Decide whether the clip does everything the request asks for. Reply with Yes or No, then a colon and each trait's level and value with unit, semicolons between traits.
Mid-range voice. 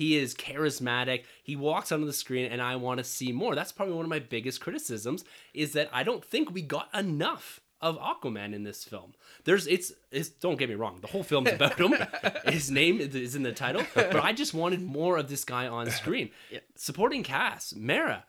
Yes: medium, 145 Hz